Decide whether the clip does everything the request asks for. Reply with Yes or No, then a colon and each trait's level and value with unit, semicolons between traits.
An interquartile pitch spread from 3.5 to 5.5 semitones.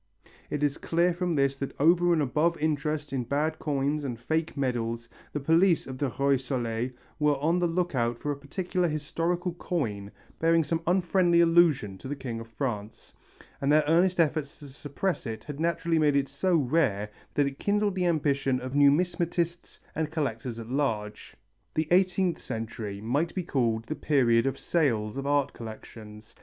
Yes: average, 5.0 semitones